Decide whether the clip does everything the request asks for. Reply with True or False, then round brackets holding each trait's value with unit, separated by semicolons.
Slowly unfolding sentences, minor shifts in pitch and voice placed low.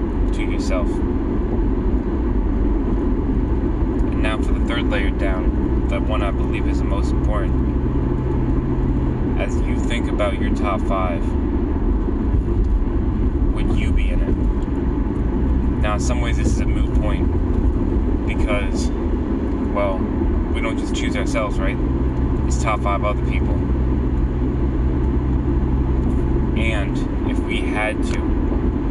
True (115 wpm; 1.3 semitones; 65 Hz)